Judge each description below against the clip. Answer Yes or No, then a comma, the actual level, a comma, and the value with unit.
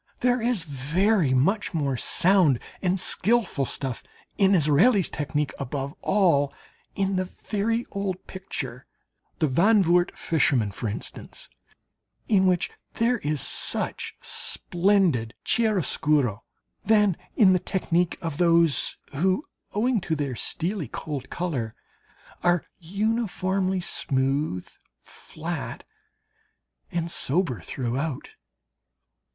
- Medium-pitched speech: Yes, medium, 175 Hz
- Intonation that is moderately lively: No, wide, 5.8 semitones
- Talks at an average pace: No, slow, 105 wpm